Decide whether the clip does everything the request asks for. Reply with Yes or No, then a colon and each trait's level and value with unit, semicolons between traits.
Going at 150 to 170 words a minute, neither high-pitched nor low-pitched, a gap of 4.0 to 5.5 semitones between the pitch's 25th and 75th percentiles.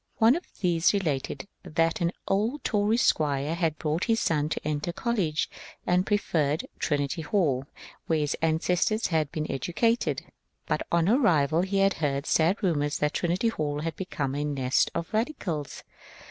Yes: average, 160 wpm; medium, 165 Hz; average, 4.8 semitones